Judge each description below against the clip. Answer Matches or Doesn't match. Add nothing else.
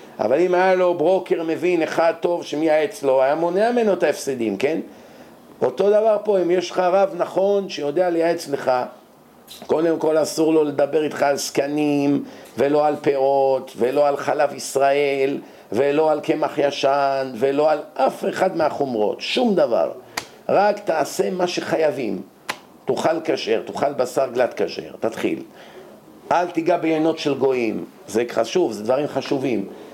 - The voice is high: Doesn't match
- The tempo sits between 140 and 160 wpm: Matches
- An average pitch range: Matches